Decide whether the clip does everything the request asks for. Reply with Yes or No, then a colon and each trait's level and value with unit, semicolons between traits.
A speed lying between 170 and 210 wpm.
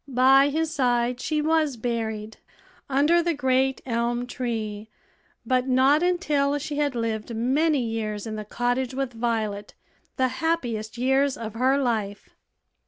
No: average, 140 wpm